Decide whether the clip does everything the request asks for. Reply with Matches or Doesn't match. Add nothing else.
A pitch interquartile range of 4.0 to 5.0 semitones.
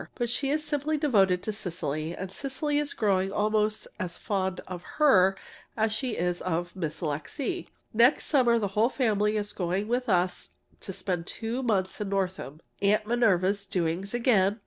Matches